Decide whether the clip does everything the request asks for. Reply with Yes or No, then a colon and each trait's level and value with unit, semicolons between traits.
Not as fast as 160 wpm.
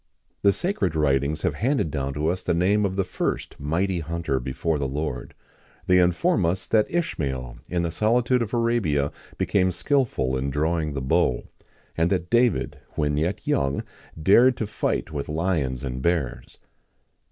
No: average, 170 wpm